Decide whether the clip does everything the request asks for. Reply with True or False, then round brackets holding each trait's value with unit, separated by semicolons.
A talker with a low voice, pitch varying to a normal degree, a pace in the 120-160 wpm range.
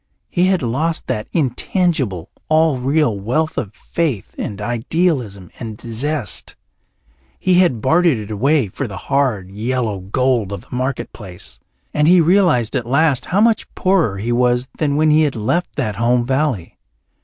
False (130 Hz; 6.2 semitones; 155 wpm)